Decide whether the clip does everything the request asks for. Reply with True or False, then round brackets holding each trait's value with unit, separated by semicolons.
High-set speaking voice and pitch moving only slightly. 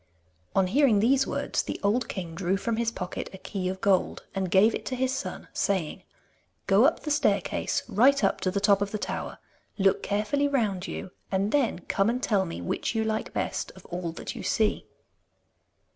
False (205 Hz; 3.8 semitones)